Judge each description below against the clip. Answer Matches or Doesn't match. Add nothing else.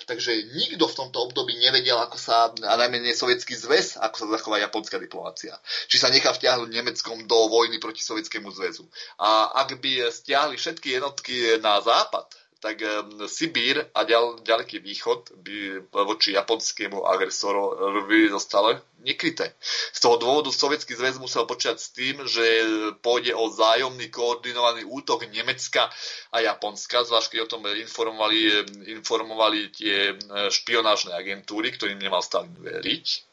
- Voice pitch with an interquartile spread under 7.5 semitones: Matches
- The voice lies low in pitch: Matches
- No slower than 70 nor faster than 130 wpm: Doesn't match